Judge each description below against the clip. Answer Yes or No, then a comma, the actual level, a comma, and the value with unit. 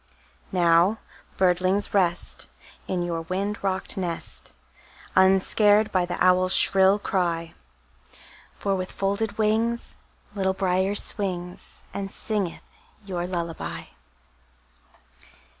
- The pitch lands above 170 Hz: Yes, high, 190 Hz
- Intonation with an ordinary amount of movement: No, narrow, 2.1 semitones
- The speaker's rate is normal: No, slow, 95 wpm